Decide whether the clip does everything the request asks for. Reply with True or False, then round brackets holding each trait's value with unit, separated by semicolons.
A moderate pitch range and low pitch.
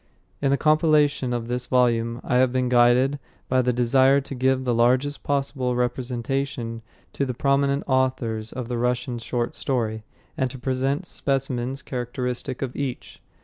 False (2.0 semitones; 130 Hz)